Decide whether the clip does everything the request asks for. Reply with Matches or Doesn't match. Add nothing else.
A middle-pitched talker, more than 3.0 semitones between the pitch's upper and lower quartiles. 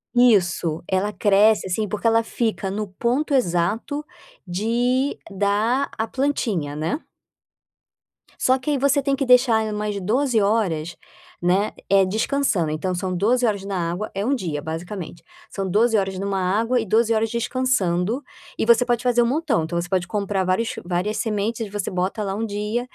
Doesn't match